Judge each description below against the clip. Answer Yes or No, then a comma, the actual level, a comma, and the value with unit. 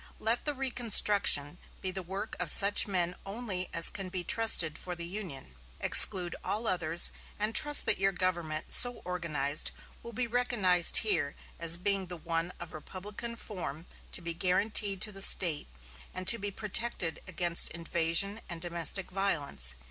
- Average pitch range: Yes, average, 3.6 semitones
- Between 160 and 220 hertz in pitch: Yes, medium, 185 Hz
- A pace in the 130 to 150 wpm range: No, average, 160 wpm